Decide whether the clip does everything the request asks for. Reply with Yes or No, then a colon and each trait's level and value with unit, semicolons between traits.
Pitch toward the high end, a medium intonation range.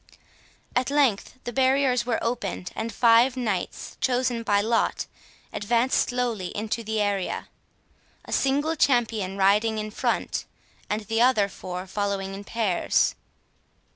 Yes: high, 225 Hz; average, 3.5 semitones